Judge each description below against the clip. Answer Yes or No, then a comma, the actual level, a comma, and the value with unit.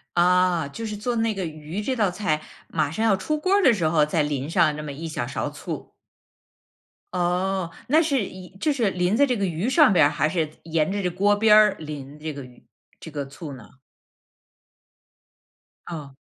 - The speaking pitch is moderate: Yes, medium, 180 Hz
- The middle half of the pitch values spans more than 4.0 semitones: Yes, wide, 5.5 semitones